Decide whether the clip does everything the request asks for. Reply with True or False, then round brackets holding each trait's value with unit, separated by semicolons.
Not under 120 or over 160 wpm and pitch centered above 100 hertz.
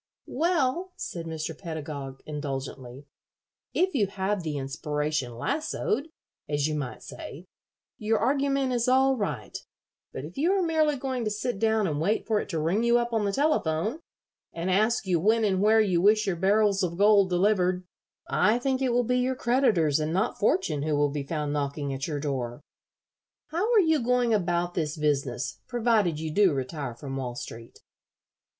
False (180 wpm; 190 Hz)